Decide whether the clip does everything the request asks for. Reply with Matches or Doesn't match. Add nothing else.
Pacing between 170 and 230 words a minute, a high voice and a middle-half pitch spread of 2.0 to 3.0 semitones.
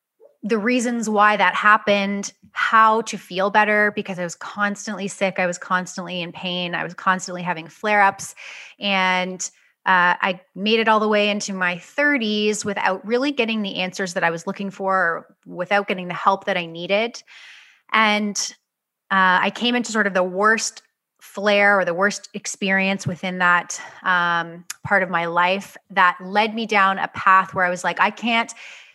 Matches